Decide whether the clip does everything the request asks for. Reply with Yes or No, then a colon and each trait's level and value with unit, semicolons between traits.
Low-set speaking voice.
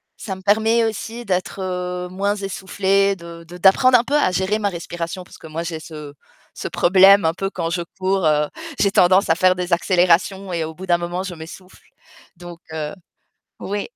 No: medium, 185 Hz